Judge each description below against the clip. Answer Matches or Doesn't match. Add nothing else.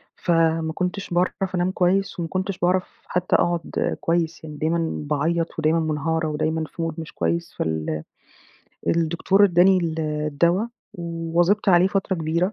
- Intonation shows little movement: Matches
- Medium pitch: Matches